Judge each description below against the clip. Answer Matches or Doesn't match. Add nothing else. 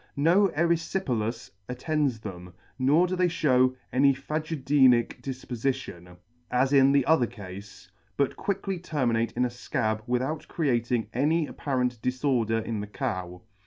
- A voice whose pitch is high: Doesn't match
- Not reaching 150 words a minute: Matches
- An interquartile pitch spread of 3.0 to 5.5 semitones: Matches